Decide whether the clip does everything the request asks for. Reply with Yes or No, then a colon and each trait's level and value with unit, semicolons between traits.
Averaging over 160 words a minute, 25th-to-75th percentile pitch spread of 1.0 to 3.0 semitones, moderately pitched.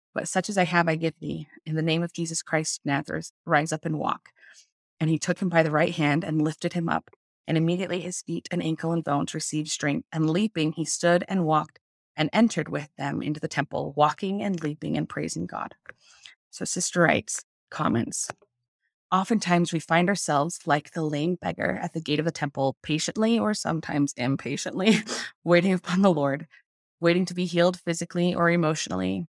Yes: average, 190 wpm; average, 2.7 semitones; medium, 165 Hz